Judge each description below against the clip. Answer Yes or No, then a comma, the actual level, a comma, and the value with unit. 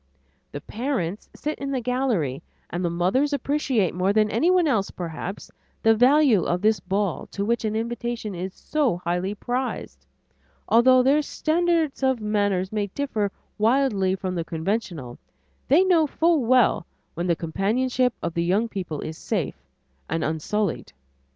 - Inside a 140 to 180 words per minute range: Yes, average, 150 wpm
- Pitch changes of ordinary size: No, wide, 6.2 semitones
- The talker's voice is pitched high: Yes, high, 215 Hz